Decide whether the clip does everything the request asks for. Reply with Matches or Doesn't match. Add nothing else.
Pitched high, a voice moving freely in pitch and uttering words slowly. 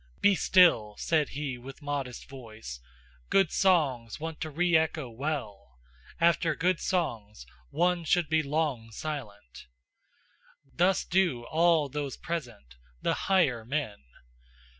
Doesn't match